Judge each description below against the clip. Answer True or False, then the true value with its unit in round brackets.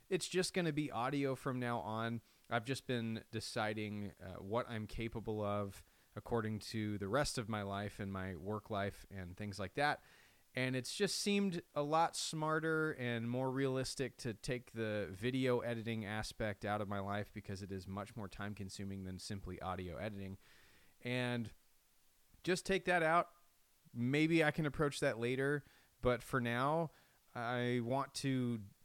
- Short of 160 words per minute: False (170 wpm)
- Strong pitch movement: False (4.9 semitones)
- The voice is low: True (120 Hz)